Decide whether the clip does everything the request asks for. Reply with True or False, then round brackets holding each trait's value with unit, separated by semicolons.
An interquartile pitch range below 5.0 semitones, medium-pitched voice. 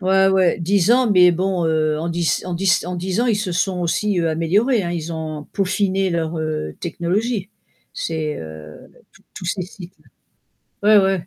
True (2.9 semitones; 180 Hz)